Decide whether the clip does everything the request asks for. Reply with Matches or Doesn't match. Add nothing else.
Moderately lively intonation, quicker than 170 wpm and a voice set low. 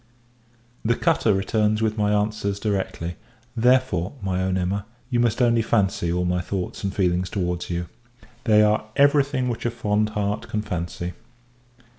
Doesn't match